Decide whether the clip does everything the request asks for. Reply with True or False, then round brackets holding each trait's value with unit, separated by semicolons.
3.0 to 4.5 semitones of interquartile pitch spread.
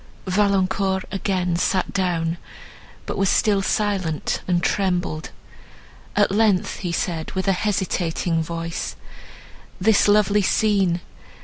False (2.5 semitones)